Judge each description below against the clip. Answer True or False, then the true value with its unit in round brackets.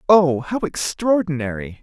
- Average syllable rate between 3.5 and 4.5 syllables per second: True (4.4 syllables/s)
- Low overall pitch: False (160 Hz)